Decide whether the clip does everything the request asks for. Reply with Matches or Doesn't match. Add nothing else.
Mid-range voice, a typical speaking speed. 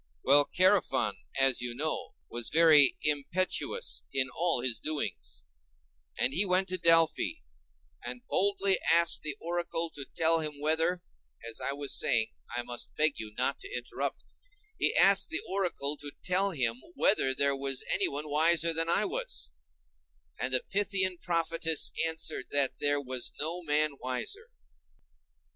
Matches